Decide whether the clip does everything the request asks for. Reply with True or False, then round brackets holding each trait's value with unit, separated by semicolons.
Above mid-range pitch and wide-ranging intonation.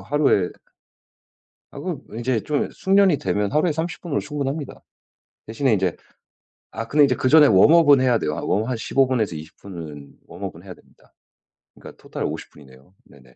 False (125 Hz; 7.7 semitones)